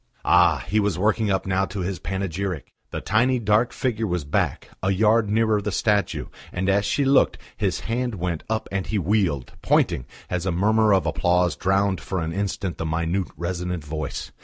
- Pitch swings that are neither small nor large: Yes, average, 3.2 semitones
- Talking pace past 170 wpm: Yes, average, 185 wpm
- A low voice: Yes, very low, 95 Hz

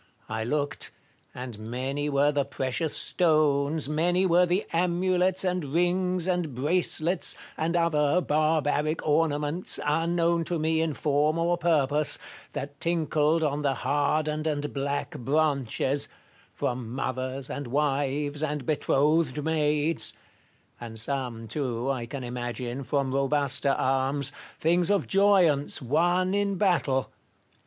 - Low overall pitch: No, medium, 150 Hz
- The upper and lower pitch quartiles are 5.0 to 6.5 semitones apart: No, average, 3.4 semitones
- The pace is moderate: No, slow, 125 wpm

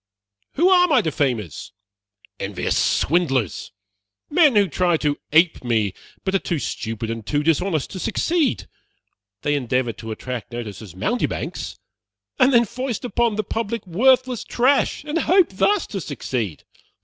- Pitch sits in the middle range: Yes, medium, 175 Hz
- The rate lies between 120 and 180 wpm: Yes, average, 145 wpm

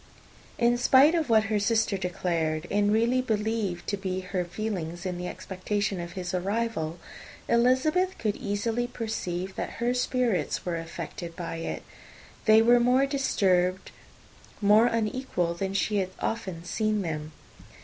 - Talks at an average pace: Yes, average, 145 wpm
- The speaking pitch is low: No, high, 205 Hz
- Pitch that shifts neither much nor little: Yes, average, 4.6 semitones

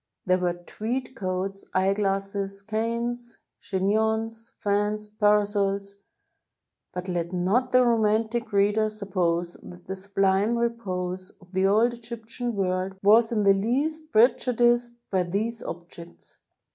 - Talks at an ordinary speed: No, slow, 125 wpm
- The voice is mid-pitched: No, high, 205 Hz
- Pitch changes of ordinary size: Yes, average, 3.3 semitones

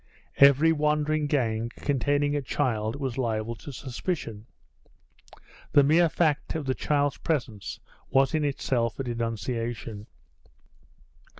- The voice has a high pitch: No, low, 135 Hz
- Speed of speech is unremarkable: No, slow, 115 wpm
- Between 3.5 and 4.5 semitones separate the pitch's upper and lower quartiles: Yes, average, 4.1 semitones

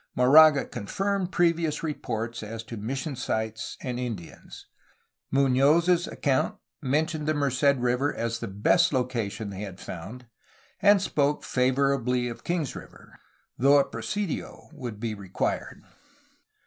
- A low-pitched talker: Yes, low, 130 Hz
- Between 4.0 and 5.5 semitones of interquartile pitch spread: Yes, average, 4.7 semitones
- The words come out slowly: Yes, slow, 130 wpm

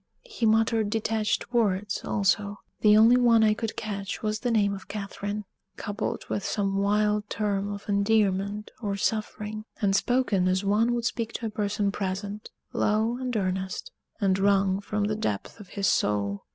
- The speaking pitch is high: Yes, high, 210 Hz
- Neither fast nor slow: Yes, average, 165 wpm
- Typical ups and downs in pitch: No, narrow, 1.7 semitones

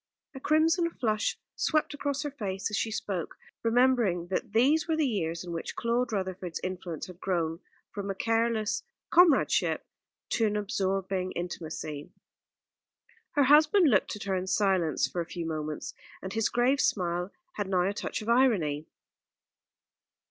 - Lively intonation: Yes, wide, 5.7 semitones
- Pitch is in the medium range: No, high, 200 Hz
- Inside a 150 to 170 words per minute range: Yes, average, 155 wpm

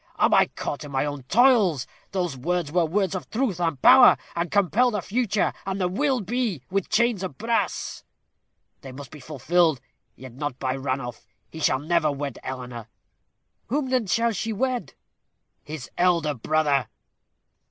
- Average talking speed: Yes, average, 165 wpm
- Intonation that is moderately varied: No, wide, 7.1 semitones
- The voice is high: No, medium, 175 Hz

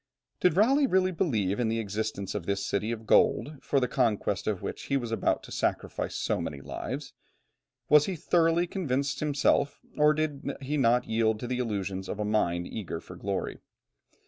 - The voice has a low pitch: Yes, low, 125 Hz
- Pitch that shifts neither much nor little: No, wide, 6.1 semitones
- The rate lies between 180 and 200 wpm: Yes, average, 185 wpm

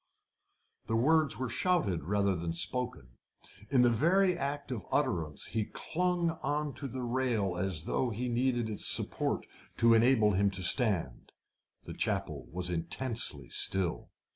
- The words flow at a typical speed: Yes, average, 145 wpm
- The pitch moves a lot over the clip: Yes, wide, 6.2 semitones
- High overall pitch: No, low, 115 Hz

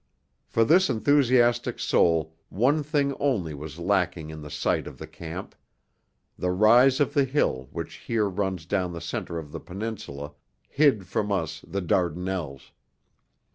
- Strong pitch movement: Yes, wide, 6.5 semitones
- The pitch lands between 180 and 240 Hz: No, very low, 95 Hz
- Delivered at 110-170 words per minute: Yes, average, 150 wpm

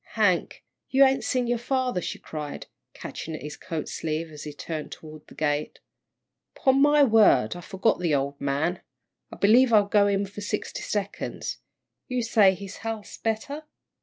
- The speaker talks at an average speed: Yes, average, 170 wpm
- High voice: Yes, high, 200 Hz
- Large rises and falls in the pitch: Yes, wide, 7.1 semitones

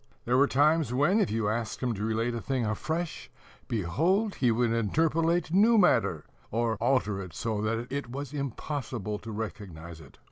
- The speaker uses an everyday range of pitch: No, wide, 5.9 semitones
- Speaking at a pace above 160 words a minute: Yes, average, 175 wpm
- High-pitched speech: No, low, 120 Hz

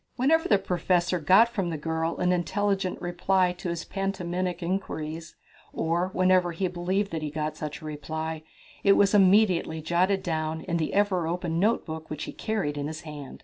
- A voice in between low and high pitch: Yes, medium, 175 Hz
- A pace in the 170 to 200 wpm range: Yes, average, 180 wpm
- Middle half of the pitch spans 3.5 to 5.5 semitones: No, average, 3.1 semitones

